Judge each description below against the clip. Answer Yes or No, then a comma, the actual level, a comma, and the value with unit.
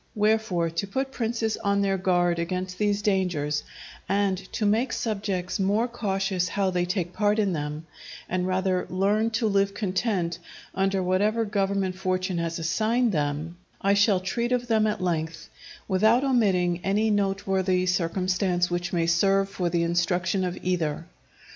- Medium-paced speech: Yes, average, 155 wpm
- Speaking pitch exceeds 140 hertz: Yes, high, 190 Hz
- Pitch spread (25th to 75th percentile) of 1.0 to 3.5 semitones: Yes, average, 2.7 semitones